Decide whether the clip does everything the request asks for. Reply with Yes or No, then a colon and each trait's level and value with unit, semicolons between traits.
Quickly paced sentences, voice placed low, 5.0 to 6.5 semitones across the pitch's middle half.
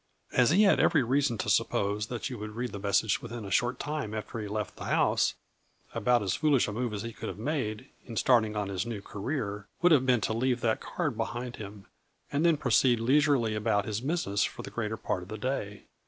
No: fast, 230 wpm; low, 115 Hz; average, 3.6 semitones